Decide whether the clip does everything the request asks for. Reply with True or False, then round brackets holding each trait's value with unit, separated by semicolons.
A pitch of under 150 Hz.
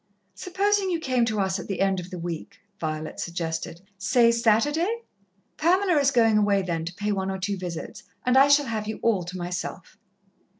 False (210 Hz)